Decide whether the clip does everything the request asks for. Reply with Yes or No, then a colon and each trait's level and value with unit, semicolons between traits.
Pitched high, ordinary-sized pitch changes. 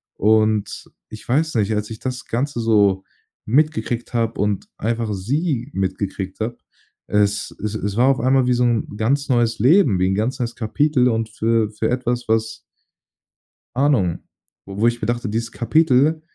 No: low, 115 Hz; average, 3.1 semitones